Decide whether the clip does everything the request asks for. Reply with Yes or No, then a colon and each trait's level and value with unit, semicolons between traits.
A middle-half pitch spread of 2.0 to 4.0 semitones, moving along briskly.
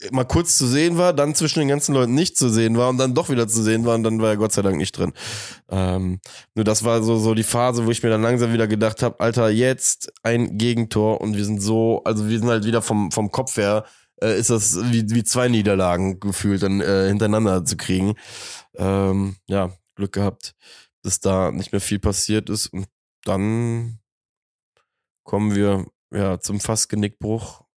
Yes: average, 2.8 semitones; fast, 205 wpm